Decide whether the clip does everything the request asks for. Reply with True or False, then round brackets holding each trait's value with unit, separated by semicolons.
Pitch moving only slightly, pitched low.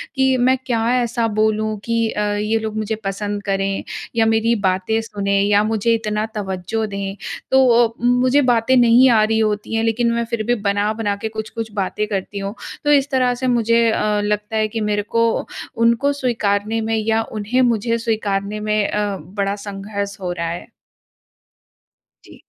False (2.2 semitones; 220 Hz)